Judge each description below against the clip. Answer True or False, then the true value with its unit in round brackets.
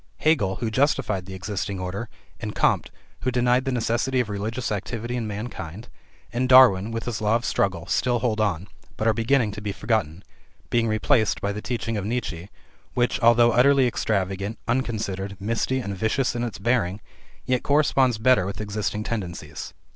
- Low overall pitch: True (110 Hz)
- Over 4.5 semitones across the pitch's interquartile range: False (3.6 semitones)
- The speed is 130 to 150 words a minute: False (170 wpm)